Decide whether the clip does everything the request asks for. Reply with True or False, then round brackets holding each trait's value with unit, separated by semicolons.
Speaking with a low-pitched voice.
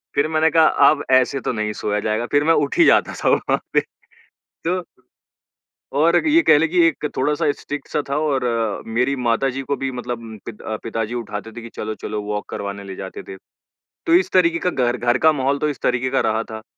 True (130 Hz)